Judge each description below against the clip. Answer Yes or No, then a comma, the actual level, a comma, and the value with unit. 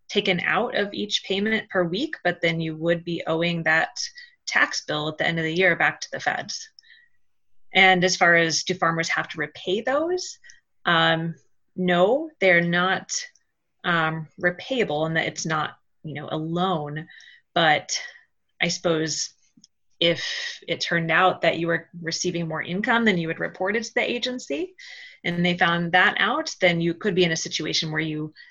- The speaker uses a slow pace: No, average, 175 wpm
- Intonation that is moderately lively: No, wide, 6.3 semitones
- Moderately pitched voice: Yes, medium, 180 Hz